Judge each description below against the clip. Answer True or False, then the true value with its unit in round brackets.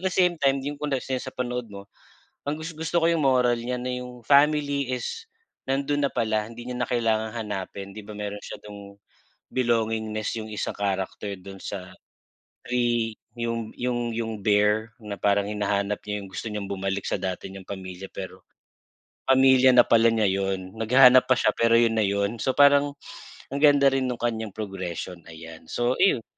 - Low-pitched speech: True (115 Hz)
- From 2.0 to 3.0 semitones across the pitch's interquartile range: False (4.2 semitones)